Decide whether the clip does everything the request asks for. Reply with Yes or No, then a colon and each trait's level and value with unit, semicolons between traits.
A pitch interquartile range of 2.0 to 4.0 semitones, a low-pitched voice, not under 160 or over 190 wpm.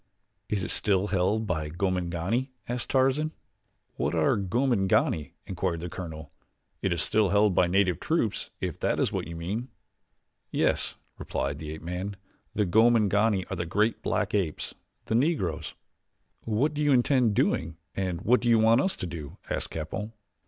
No: average, 4.8 semitones; low, 100 Hz; average, 165 wpm